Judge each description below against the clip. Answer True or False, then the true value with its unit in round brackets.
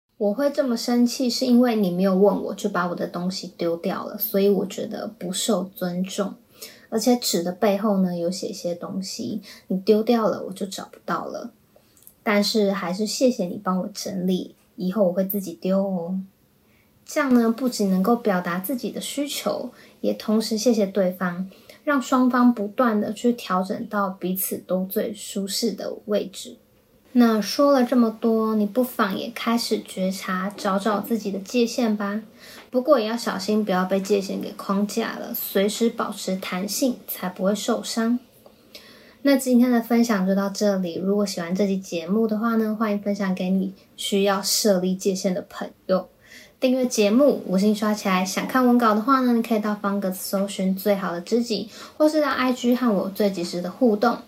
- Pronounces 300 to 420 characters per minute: False (265 characters per minute)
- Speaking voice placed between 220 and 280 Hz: False (210 Hz)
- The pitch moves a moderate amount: True (3.4 semitones)